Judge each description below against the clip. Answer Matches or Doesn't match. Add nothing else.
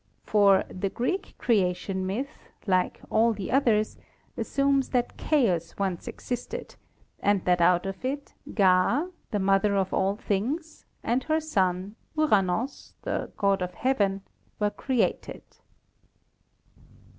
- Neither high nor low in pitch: Doesn't match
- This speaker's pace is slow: Matches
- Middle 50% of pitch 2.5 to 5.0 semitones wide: Doesn't match